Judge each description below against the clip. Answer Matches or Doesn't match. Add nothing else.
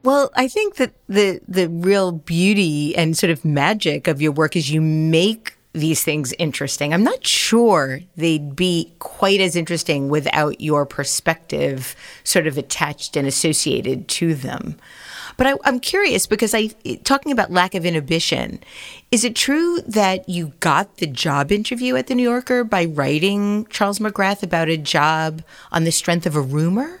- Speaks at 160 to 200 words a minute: Matches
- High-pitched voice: Doesn't match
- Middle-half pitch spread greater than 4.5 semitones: Matches